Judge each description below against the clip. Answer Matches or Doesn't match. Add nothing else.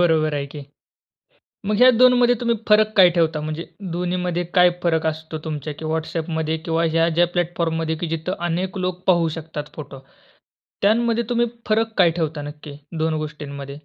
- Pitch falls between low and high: Matches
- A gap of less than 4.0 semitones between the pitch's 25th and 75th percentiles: Matches